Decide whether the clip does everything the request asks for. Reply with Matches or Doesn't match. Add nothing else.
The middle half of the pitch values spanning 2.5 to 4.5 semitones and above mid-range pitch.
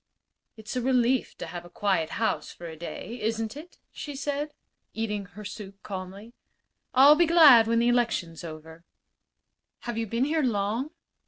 Doesn't match